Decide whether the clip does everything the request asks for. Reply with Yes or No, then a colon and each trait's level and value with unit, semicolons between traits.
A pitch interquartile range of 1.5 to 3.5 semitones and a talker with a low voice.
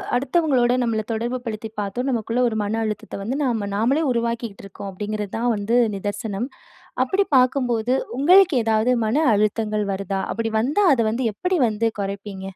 No: average, 3.2 semitones; high, 225 Hz